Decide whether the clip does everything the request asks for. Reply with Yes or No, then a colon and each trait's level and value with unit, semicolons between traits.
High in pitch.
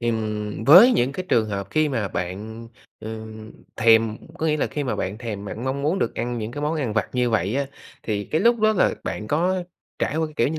No: low, 115 Hz